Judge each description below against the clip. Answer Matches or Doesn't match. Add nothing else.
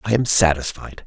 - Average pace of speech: Matches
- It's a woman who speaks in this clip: Doesn't match